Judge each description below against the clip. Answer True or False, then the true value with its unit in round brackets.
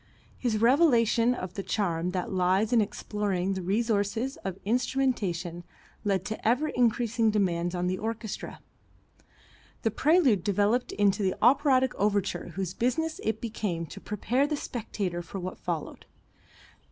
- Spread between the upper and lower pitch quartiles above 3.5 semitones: True (4.4 semitones)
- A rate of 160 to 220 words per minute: False (140 wpm)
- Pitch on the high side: True (210 Hz)